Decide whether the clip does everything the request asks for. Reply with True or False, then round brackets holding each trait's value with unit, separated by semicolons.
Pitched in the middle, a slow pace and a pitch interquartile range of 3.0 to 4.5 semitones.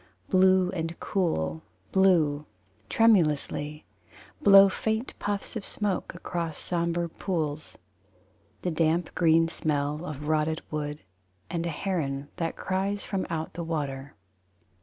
True (165 Hz; 115 wpm; 3.7 semitones)